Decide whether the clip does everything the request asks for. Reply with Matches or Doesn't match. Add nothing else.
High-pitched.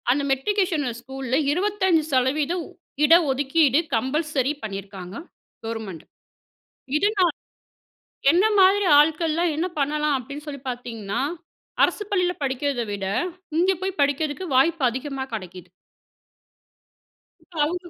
Matches